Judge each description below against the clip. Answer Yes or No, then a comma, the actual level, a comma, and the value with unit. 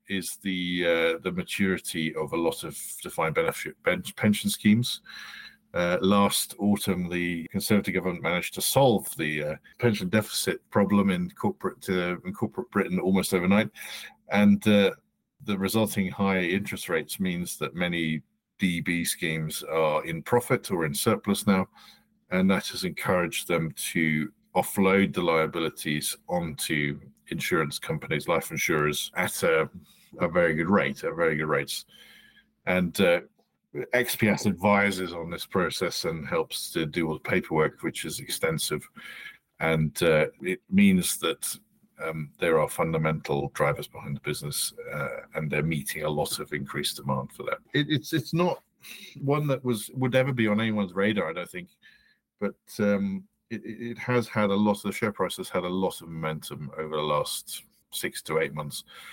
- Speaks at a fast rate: No, average, 160 wpm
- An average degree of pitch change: Yes, average, 4.3 semitones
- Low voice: Yes, very low, 95 Hz